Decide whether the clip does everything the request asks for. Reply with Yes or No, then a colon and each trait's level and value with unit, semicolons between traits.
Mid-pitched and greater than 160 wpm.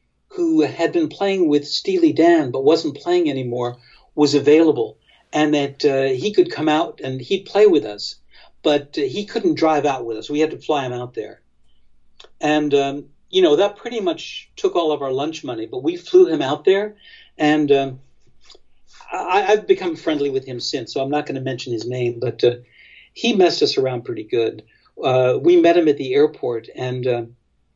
Yes: medium, 150 Hz; average, 200 wpm